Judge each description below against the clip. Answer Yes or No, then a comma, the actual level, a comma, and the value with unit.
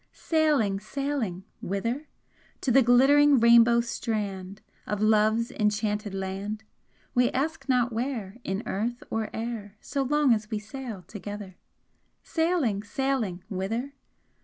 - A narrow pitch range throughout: No, average, 4.2 semitones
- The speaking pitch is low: No, high, 225 Hz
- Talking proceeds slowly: Yes, slow, 120 wpm